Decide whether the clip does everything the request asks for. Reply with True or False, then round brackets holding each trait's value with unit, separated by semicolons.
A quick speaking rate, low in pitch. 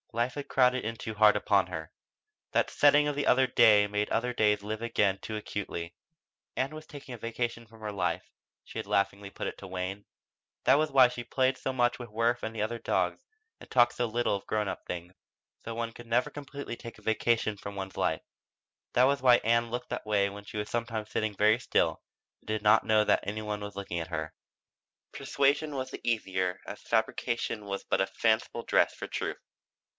True (210 wpm; 110 Hz)